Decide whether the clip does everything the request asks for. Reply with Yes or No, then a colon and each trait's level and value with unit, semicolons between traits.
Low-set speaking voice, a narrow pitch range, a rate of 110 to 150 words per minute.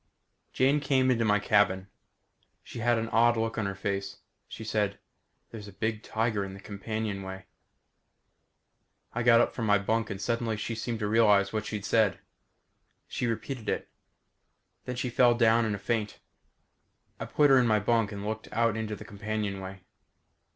No: low, 110 Hz; narrow, 2.3 semitones; average, 170 wpm